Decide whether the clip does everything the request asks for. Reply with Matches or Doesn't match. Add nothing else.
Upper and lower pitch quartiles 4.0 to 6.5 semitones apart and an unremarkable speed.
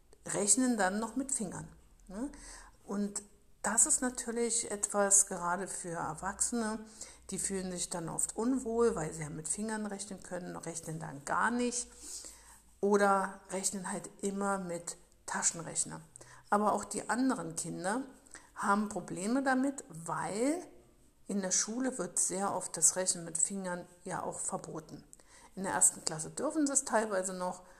Matches